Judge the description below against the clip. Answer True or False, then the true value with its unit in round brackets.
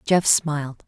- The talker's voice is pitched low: False (150 Hz)